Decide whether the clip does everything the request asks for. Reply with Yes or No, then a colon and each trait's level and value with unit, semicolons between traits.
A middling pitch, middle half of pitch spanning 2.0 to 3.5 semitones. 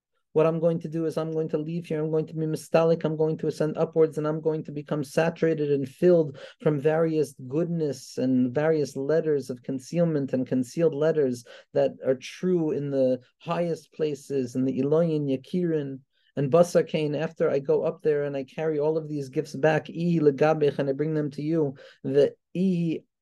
Yes: medium, 155 Hz; narrow, 2.4 semitones